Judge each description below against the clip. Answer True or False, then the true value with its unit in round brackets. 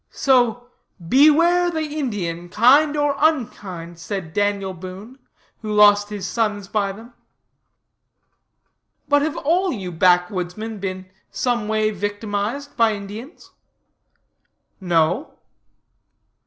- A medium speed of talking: False (100 wpm)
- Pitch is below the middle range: False (210 Hz)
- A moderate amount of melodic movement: False (5.8 semitones)